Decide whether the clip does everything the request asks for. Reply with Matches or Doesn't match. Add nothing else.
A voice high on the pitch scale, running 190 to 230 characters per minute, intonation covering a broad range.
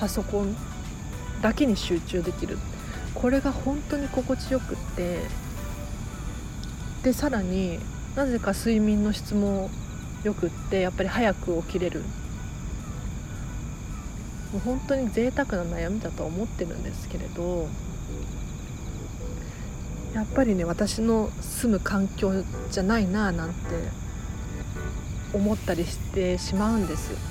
Doesn't match